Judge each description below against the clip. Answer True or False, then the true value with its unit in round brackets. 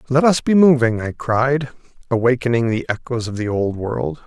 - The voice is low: True (125 Hz)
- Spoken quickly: False (185 wpm)